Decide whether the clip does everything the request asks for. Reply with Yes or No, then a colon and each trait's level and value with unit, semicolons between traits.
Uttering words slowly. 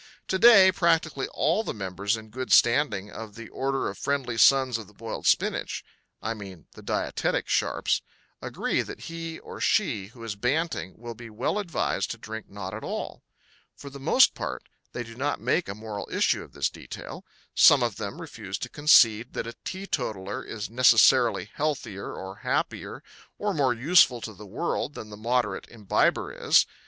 No: average, 180 wpm